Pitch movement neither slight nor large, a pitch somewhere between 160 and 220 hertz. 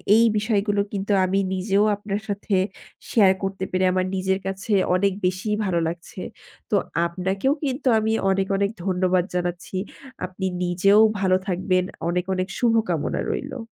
No: narrow, 1.8 semitones; high, 190 Hz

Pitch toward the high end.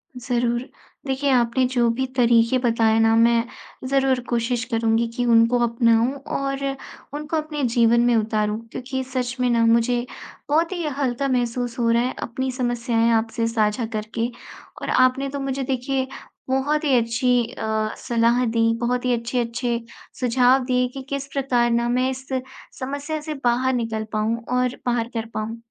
Yes: high, 245 Hz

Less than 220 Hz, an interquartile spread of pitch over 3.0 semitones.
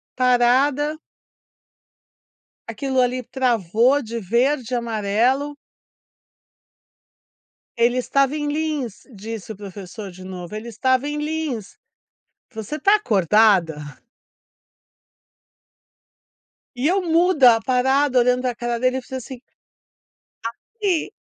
No: very high, 250 Hz; average, 4.4 semitones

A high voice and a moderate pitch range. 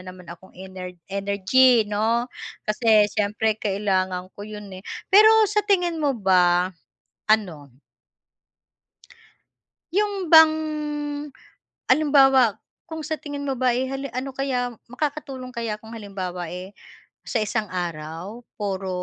No: high, 215 Hz; wide, 6.2 semitones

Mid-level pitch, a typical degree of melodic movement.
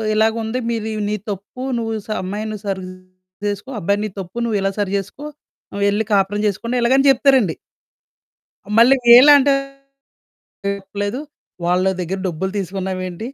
No: high, 205 Hz; average, 3.5 semitones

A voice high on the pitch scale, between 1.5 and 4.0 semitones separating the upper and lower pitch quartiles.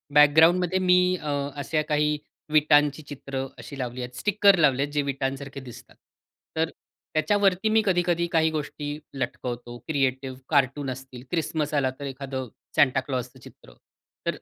No: medium, 145 Hz; average, 3.3 semitones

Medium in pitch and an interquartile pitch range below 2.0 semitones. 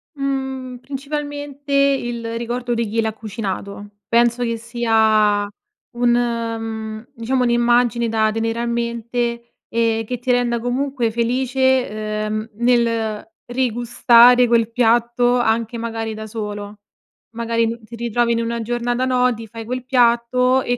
No: high, 235 Hz; narrow, 1.6 semitones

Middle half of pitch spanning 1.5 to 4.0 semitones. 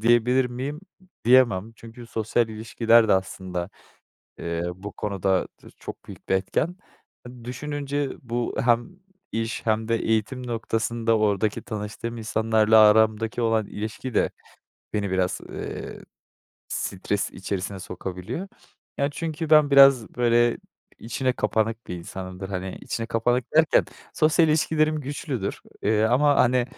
Yes: average, 3.4 semitones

